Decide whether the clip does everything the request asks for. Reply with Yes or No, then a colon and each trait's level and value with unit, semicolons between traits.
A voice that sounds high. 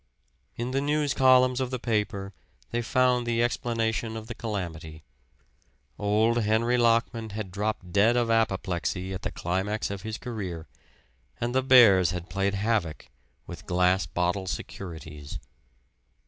No: low, 110 Hz